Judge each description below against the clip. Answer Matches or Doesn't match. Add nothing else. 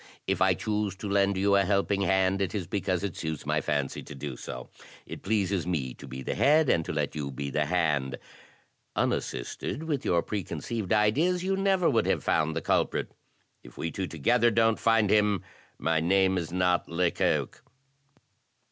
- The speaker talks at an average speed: Matches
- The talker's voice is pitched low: Matches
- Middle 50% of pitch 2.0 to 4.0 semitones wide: Doesn't match